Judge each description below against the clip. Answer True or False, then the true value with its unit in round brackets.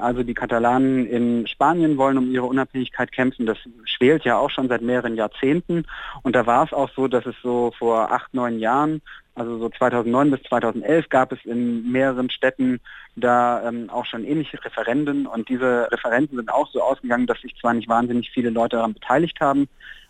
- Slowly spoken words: False (190 wpm)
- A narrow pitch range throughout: True (2.1 semitones)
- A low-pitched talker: True (125 Hz)